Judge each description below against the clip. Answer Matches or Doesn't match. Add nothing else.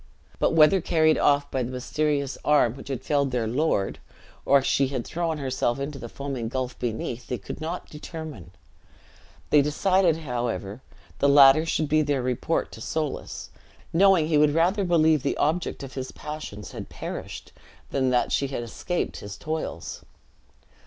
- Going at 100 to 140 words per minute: Doesn't match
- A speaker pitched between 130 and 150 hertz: Matches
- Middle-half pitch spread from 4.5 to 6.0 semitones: Doesn't match